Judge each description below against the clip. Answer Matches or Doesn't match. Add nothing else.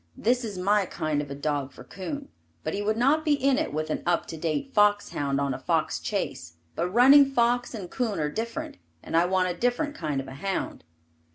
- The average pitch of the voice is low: Doesn't match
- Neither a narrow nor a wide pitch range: Doesn't match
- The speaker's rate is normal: Doesn't match